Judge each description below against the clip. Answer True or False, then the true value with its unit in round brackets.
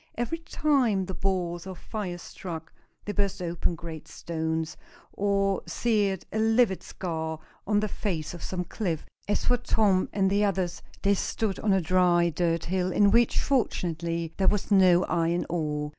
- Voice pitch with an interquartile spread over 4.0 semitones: False (3.3 semitones)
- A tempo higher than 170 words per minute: False (165 wpm)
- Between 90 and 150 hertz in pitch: False (185 Hz)